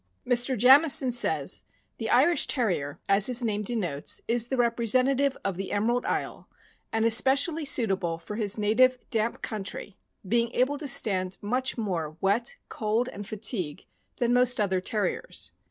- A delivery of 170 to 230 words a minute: No, average, 150 wpm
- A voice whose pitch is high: Yes, high, 230 Hz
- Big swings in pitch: No, average, 3.8 semitones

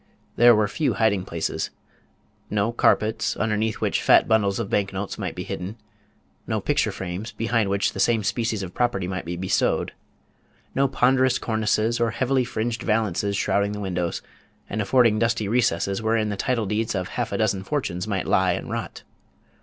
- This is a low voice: Yes, low, 110 Hz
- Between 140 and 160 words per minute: No, average, 175 wpm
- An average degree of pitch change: Yes, average, 3.0 semitones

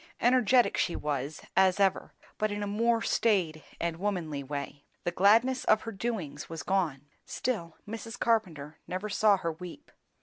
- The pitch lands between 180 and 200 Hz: Yes, high, 190 Hz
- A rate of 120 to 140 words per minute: No, average, 160 wpm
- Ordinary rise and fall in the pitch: No, wide, 5.7 semitones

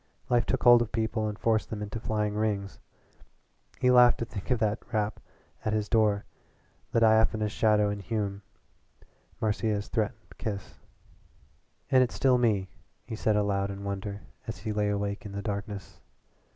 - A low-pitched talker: Yes, low, 105 Hz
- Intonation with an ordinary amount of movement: No, narrow, 1.6 semitones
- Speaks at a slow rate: No, average, 165 wpm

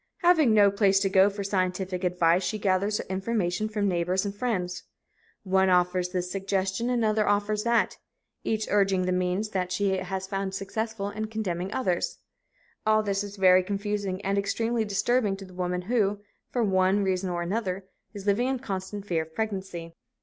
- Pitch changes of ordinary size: No, narrow, 2.3 semitones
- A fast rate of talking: No, average, 175 wpm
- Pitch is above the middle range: Yes, high, 195 Hz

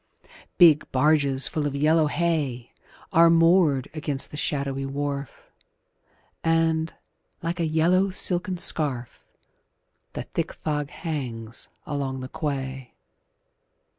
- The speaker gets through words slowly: Yes, slow, 105 wpm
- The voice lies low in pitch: No, medium, 150 Hz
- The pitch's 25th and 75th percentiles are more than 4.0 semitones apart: No, average, 3.2 semitones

